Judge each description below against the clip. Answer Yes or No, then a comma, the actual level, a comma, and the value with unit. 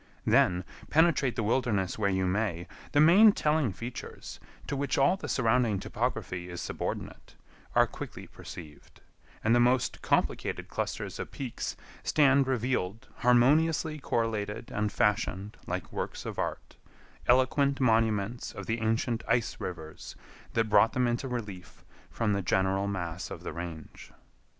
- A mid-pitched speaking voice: No, low, 115 Hz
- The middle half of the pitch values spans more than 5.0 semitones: No, average, 4.6 semitones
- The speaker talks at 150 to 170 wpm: No, average, 140 wpm